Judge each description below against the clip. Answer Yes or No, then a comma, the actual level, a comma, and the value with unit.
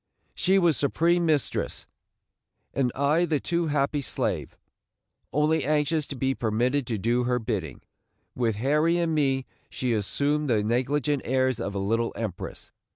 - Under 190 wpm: Yes, average, 150 wpm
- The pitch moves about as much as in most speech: Yes, average, 4.2 semitones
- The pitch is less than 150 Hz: Yes, low, 135 Hz